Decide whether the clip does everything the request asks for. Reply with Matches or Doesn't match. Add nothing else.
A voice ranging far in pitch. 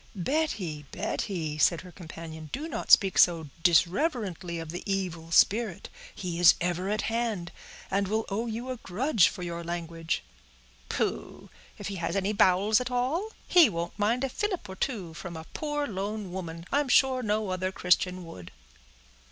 Doesn't match